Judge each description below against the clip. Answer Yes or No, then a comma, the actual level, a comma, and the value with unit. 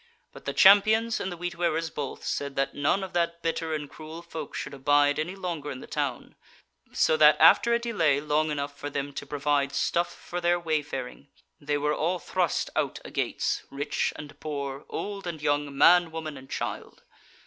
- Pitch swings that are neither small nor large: Yes, average, 3.4 semitones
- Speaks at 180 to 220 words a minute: Yes, average, 190 wpm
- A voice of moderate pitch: Yes, medium, 155 Hz